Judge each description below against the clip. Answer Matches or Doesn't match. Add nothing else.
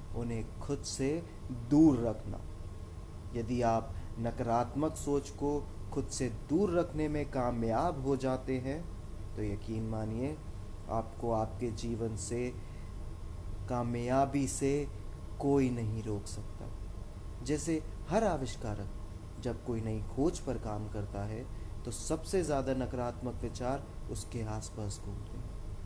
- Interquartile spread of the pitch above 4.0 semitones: Matches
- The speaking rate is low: Doesn't match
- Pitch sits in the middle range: Doesn't match